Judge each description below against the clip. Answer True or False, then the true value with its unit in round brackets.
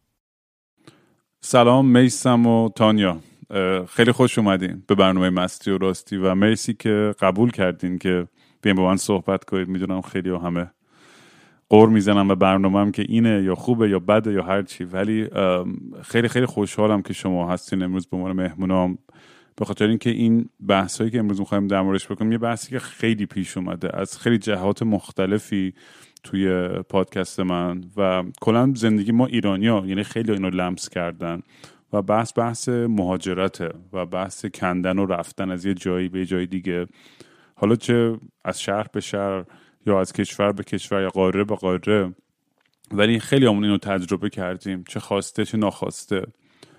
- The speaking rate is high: True (160 wpm)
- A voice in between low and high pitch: False (100 Hz)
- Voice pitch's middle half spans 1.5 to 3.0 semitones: True (2.7 semitones)